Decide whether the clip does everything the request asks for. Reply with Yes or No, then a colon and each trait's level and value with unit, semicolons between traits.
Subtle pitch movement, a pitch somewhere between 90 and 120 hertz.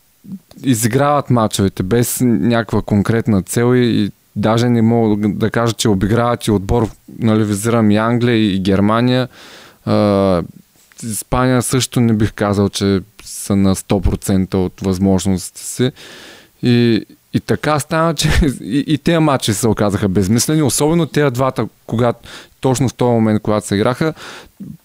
No: average, 3.5 semitones; low, 115 Hz